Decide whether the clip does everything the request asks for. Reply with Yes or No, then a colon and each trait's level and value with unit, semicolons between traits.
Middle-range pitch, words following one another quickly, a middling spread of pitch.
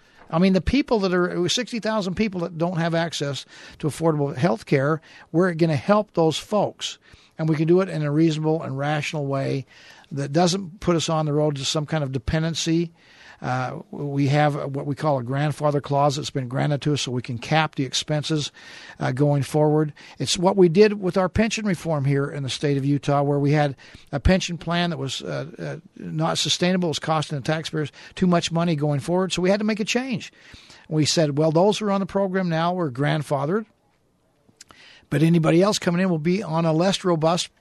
Yes: medium, 160 Hz; fast, 215 wpm; average, 3.6 semitones